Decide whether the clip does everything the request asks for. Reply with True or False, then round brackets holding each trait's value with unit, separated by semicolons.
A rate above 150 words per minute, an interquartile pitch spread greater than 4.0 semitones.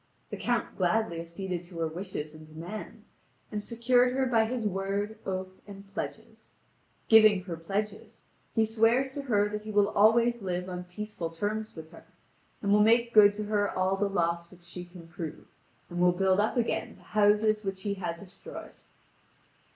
False (180 wpm; 3.4 semitones)